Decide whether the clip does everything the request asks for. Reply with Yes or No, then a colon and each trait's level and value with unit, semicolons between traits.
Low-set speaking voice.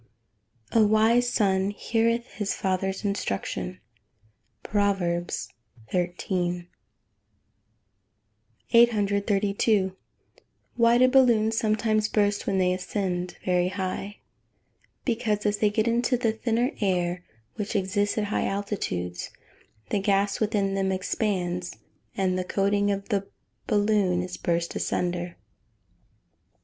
No: high, 200 Hz